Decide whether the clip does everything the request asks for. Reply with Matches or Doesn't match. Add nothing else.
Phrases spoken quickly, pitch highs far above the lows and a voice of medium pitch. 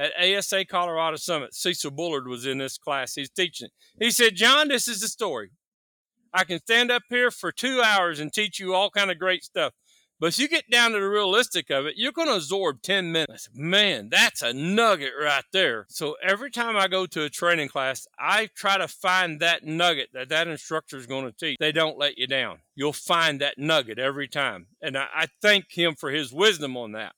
Matches